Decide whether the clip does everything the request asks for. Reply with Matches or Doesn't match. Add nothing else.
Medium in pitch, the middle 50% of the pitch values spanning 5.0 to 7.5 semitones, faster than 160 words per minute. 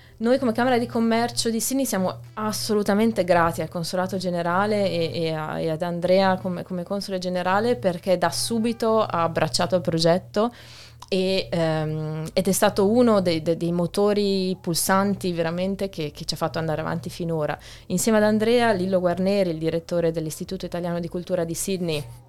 Doesn't match